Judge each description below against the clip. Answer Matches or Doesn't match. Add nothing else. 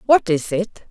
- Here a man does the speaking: Doesn't match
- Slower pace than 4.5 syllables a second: Matches